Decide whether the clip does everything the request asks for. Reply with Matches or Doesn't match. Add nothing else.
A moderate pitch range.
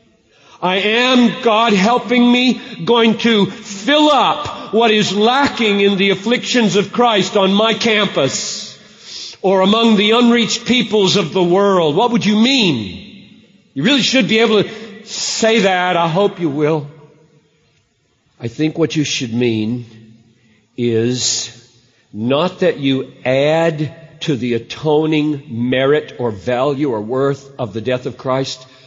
Doesn't match